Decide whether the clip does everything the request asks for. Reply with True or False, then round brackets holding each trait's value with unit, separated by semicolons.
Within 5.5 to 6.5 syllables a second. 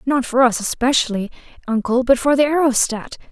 True (5.6 syllables/s)